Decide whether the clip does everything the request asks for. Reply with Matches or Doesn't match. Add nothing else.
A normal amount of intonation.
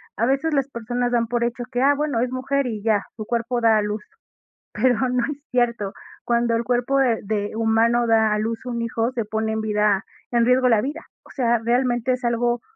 Doesn't match